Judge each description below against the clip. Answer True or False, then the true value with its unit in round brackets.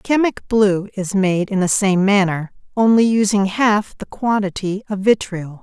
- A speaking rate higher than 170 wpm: False (160 wpm)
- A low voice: False (200 Hz)